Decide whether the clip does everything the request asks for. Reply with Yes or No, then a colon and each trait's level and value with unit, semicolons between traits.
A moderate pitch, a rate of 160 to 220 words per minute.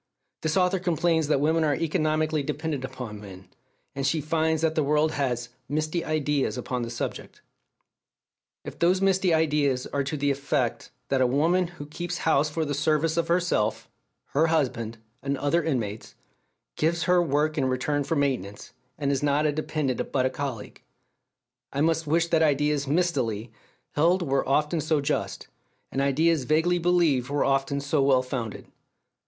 Yes: medium, 150 Hz; average, 170 wpm